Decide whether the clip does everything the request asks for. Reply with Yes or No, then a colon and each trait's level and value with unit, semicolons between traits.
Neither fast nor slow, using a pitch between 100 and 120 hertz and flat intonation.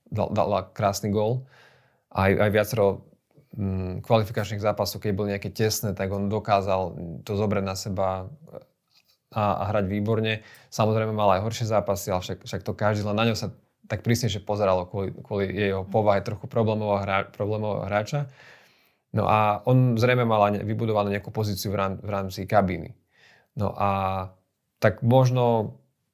Yes: average, 155 wpm; low, 105 Hz; narrow, 2.0 semitones